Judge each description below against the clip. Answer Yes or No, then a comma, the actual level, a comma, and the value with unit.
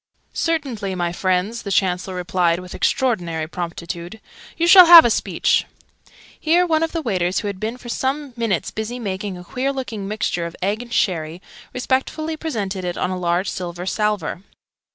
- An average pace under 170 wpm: No, average, 175 wpm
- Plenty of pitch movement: Yes, wide, 5.9 semitones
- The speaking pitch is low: No, high, 200 Hz